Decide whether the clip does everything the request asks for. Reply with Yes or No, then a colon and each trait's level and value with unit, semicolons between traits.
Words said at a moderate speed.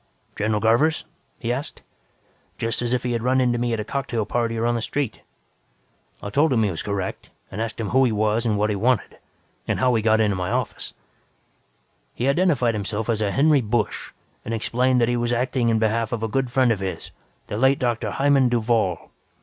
No: fast, 215 wpm